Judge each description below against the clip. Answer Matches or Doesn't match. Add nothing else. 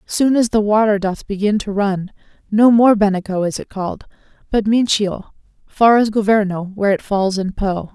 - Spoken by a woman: Matches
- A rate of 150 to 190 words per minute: Matches